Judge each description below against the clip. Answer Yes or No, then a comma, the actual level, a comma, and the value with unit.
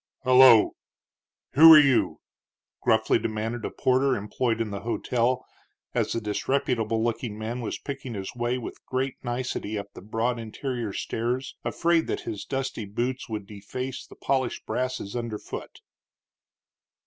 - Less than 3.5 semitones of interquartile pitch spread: Yes, average, 2.9 semitones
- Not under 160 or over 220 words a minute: No, average, 145 wpm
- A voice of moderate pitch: No, low, 120 Hz